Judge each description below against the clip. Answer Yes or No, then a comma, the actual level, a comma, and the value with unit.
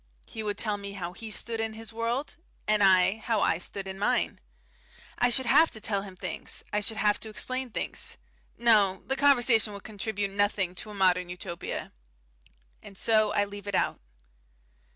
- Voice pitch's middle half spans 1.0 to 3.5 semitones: Yes, narrow, 2.4 semitones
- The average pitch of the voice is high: Yes, high, 210 Hz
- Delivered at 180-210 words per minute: Yes, average, 185 wpm